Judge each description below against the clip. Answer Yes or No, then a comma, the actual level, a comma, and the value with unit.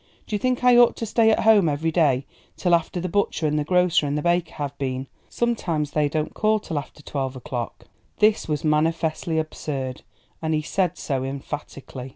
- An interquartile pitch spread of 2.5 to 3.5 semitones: No, average, 4.2 semitones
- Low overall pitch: No, medium, 155 Hz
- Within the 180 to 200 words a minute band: Yes, average, 190 wpm